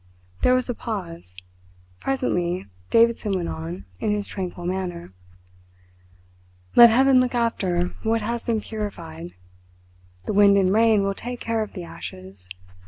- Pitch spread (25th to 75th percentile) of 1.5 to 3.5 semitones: No, average, 4.8 semitones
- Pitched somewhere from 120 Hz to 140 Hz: No, high, 200 Hz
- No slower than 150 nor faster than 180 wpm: No, average, 140 wpm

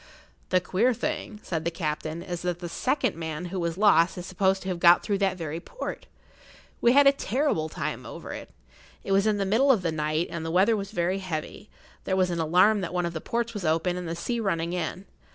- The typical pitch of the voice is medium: Yes, medium, 180 Hz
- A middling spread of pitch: Yes, average, 3.4 semitones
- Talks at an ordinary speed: No, fast, 235 wpm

